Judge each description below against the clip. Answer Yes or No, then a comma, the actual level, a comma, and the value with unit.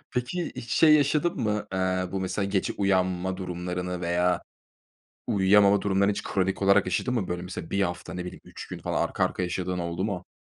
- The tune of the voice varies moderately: No, narrow, 2.1 semitones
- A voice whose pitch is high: No, very low, 95 Hz